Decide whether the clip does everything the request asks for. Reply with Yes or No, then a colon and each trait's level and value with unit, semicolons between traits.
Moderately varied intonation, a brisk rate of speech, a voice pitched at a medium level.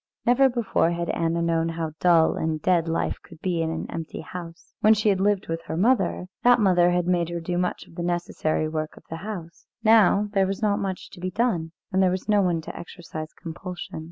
Yes: average, 3.1 semitones; fast, 225 wpm; medium, 175 Hz